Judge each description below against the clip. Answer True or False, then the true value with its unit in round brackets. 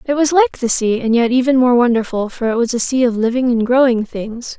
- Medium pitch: False (240 Hz)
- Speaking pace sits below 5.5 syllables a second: False (5.6 syllables/s)